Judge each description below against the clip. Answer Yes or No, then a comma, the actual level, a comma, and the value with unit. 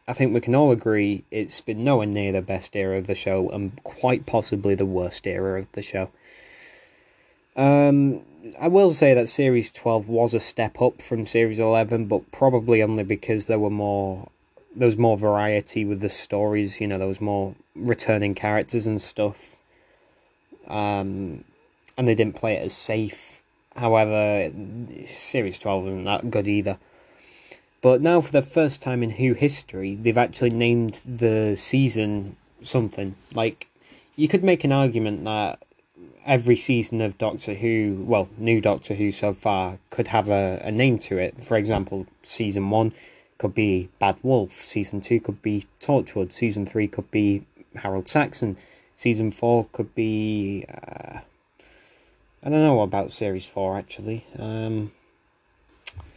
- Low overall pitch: Yes, low, 110 Hz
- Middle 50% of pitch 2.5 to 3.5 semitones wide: Yes, average, 2.9 semitones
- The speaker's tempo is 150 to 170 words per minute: Yes, average, 160 wpm